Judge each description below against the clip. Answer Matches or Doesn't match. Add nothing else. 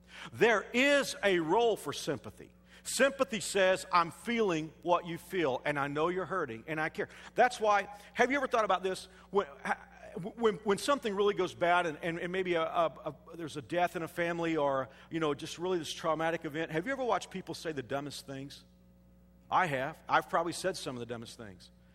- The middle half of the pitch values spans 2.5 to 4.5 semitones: Doesn't match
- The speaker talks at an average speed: Doesn't match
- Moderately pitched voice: Matches